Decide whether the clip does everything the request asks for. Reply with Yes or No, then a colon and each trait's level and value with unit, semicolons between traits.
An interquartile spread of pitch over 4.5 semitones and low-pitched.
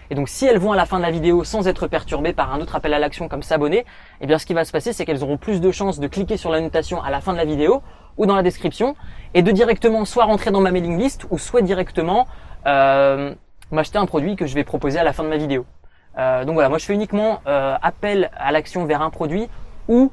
No: average, 5.0 semitones; medium, 170 Hz